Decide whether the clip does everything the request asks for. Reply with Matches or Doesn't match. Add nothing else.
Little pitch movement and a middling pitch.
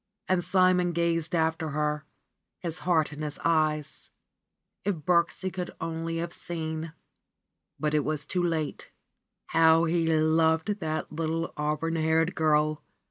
Matches